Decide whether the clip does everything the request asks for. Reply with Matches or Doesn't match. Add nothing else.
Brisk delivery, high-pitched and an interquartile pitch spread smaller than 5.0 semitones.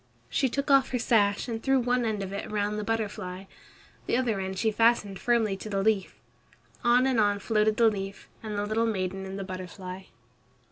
Doesn't match